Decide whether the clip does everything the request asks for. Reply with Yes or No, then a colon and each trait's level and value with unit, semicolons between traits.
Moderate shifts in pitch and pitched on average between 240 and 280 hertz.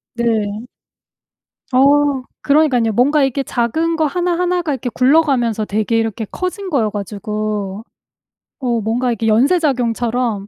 Yes: average, 4.9 semitones; high, 245 Hz